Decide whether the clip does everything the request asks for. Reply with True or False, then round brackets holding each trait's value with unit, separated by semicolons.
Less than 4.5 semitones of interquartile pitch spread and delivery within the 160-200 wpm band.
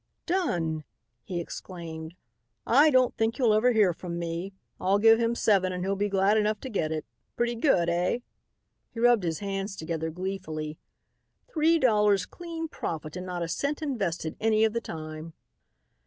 False (5.3 semitones; 170 wpm)